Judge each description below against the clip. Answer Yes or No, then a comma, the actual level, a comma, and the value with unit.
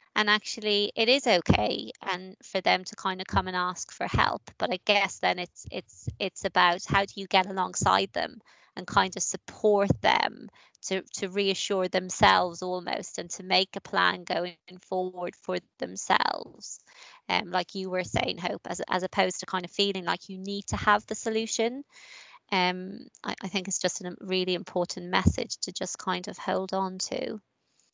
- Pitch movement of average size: No, narrow, 1.7 semitones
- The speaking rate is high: No, average, 185 wpm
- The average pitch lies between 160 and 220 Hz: Yes, high, 190 Hz